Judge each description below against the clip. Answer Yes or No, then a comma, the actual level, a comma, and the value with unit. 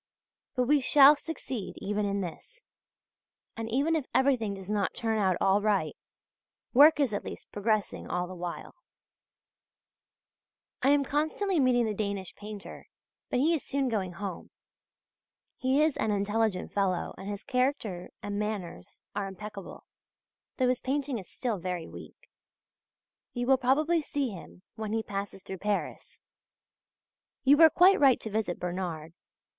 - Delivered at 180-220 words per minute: No, average, 150 wpm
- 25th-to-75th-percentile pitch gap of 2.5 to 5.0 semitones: No, wide, 5.6 semitones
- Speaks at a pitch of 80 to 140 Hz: No, high, 215 Hz